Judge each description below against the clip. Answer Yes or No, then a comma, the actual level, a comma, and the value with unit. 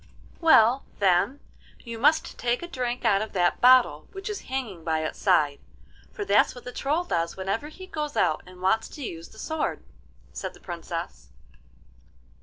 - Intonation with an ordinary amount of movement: No, wide, 8.3 semitones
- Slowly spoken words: No, average, 175 wpm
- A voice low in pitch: No, high, 225 Hz